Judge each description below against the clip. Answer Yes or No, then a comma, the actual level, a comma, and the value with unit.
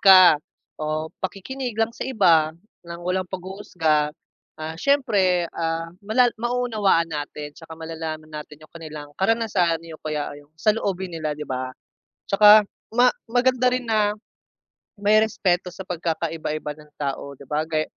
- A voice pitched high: No, medium, 175 Hz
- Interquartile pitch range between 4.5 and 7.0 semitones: Yes, average, 5.2 semitones